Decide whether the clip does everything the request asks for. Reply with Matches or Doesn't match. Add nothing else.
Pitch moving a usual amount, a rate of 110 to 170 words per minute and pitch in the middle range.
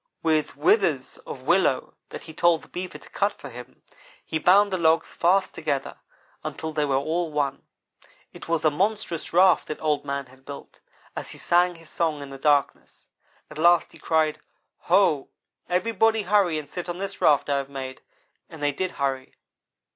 Doesn't match